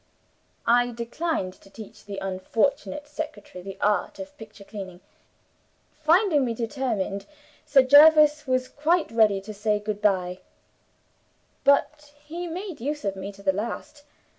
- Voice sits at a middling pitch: No, high, 235 Hz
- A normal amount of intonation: No, wide, 6.7 semitones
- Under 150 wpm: Yes, average, 140 wpm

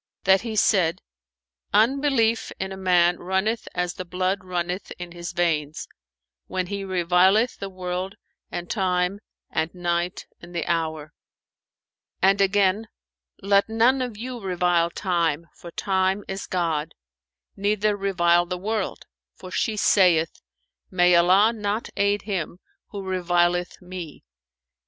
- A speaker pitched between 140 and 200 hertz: Yes, medium, 185 Hz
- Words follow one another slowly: Yes, slow, 130 wpm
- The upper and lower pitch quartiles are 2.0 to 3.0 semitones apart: Yes, narrow, 2.5 semitones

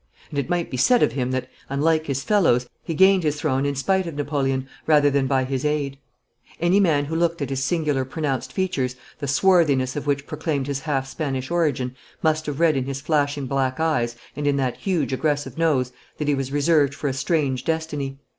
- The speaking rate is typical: No, fast, 210 wpm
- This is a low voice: No, medium, 145 Hz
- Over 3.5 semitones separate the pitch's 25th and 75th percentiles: No, average, 3.0 semitones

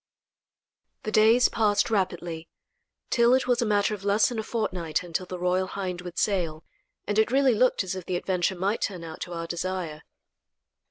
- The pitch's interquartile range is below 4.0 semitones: Yes, average, 3.5 semitones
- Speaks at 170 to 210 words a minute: Yes, average, 185 wpm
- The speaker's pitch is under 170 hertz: No, high, 190 Hz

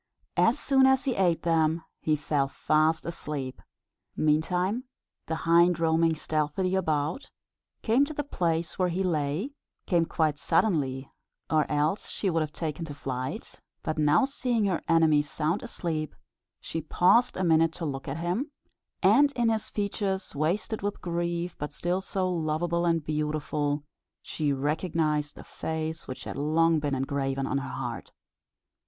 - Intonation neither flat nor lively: Yes, average, 3.4 semitones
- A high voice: No, medium, 160 Hz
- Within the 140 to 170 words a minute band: Yes, average, 155 wpm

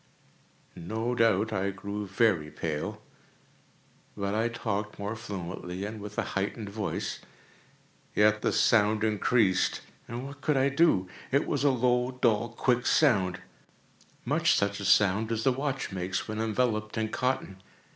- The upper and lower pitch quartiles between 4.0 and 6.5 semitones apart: No, average, 3.6 semitones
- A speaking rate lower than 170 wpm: Yes, average, 140 wpm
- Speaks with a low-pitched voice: Yes, low, 110 Hz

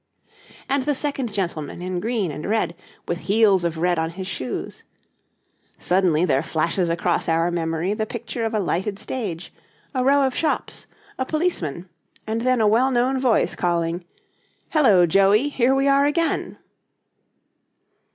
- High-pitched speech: Yes, high, 200 Hz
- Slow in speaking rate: No, average, 150 wpm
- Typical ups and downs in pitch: No, wide, 6.8 semitones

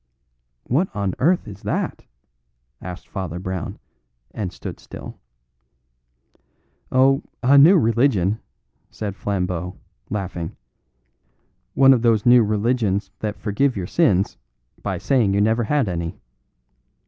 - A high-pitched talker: No, low, 105 Hz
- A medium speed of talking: No, slow, 115 wpm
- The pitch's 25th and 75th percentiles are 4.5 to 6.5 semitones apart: Yes, average, 5.3 semitones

